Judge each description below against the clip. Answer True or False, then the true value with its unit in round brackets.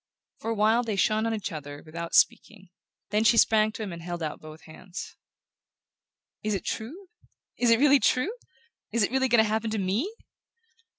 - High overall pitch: True (215 Hz)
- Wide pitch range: False (4.1 semitones)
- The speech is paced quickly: False (190 wpm)